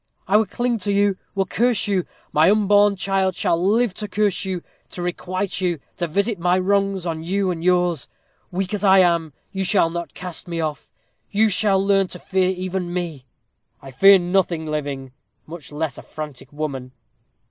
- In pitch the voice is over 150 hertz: Yes, medium, 185 Hz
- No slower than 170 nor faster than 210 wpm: Yes, average, 180 wpm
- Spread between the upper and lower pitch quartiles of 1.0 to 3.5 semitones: Yes, average, 2.9 semitones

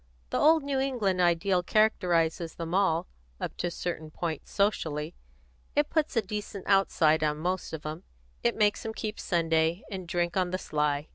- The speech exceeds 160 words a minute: Yes, average, 180 wpm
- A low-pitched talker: No, medium, 180 Hz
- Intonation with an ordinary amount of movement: Yes, average, 4.2 semitones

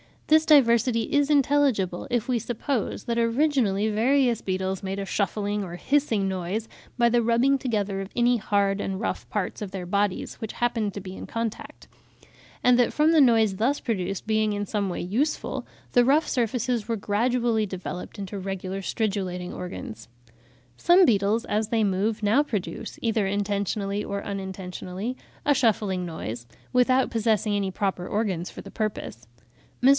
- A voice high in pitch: Yes, high, 215 Hz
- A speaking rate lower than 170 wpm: Yes, average, 160 wpm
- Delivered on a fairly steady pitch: No, average, 3.8 semitones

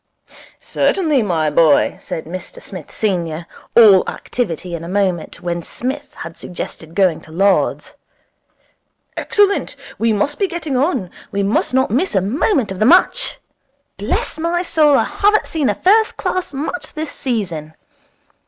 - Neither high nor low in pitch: No, high, 215 Hz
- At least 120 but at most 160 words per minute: Yes, average, 150 wpm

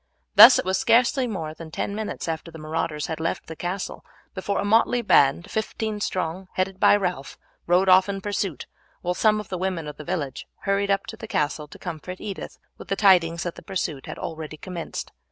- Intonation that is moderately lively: Yes, average, 3.7 semitones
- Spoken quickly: Yes, fast, 210 wpm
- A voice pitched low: No, medium, 185 Hz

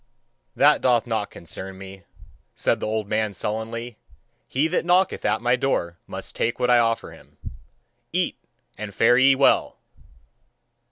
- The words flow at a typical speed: Yes, average, 150 wpm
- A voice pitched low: Yes, low, 115 Hz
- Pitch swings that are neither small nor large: Yes, average, 3.3 semitones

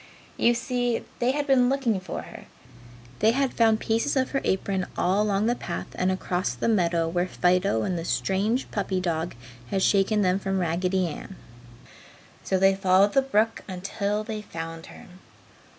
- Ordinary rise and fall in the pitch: Yes, average, 3.8 semitones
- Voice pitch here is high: Yes, high, 195 Hz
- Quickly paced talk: No, average, 170 wpm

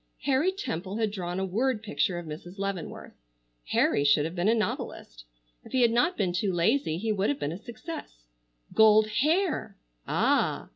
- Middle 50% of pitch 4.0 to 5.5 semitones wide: Yes, average, 5.1 semitones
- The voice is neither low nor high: No, high, 200 Hz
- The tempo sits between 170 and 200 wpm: Yes, average, 180 wpm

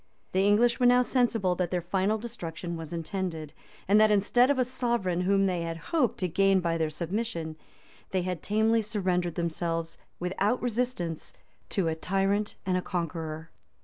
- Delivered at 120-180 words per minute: Yes, average, 175 wpm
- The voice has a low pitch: No, high, 190 Hz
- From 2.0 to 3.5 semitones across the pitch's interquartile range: No, average, 4.3 semitones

